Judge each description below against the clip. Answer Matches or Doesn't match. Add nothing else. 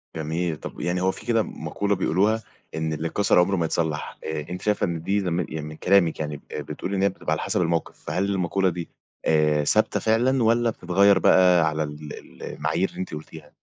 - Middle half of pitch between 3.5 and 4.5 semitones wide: Matches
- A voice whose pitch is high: Doesn't match